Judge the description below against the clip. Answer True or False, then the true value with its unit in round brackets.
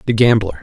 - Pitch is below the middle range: True (110 Hz)